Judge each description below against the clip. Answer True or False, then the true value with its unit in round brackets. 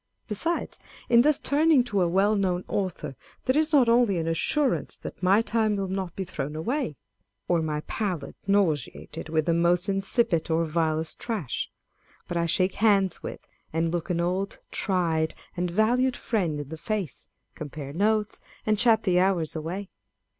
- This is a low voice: False (185 Hz)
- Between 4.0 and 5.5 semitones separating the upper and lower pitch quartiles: True (4.8 semitones)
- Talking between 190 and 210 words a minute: False (175 wpm)